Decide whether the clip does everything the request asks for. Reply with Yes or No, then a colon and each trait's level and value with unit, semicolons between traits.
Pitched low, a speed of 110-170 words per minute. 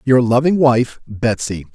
Yes: low, 120 Hz; average, 140 wpm